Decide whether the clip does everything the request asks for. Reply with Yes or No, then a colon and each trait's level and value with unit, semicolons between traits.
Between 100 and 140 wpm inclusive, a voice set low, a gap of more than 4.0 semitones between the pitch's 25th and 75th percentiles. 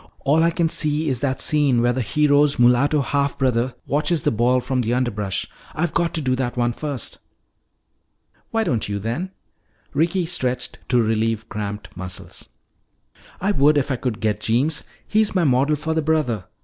No: average, 175 wpm; low, 130 Hz; average, 4.4 semitones